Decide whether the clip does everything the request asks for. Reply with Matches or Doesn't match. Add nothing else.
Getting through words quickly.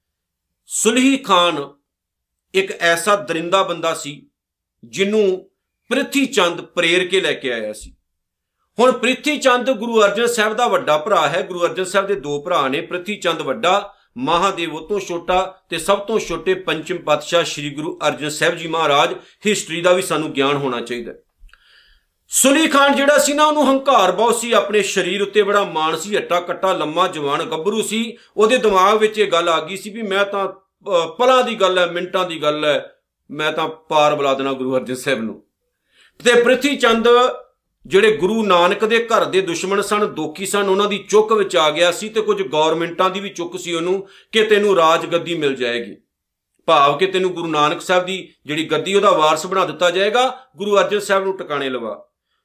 Matches